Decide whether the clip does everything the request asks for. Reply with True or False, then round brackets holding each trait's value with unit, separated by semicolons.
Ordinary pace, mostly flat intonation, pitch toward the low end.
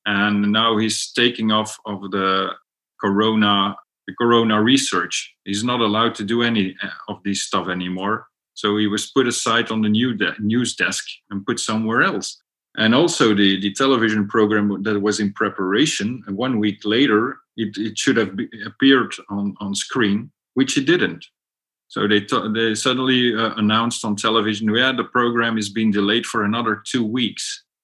True (160 wpm; 2.2 semitones; 110 Hz)